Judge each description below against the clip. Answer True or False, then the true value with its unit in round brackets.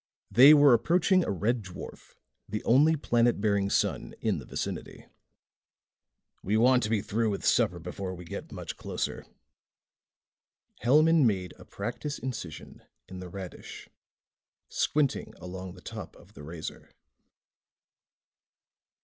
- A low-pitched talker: True (110 Hz)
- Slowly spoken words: True (130 wpm)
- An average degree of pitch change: False (5.9 semitones)